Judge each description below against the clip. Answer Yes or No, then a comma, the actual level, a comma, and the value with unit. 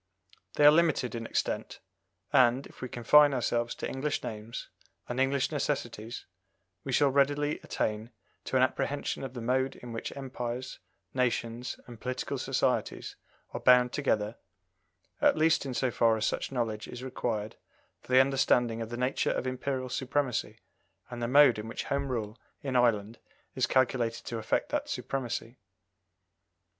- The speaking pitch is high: No, low, 125 Hz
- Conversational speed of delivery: Yes, average, 155 wpm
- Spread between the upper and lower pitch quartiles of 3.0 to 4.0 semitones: No, narrow, 2.4 semitones